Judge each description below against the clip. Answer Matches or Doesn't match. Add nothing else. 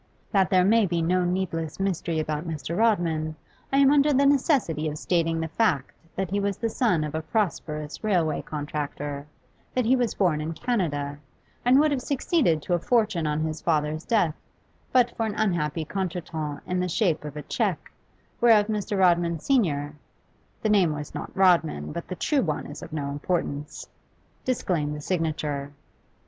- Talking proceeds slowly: Doesn't match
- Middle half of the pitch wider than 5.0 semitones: Matches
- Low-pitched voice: Doesn't match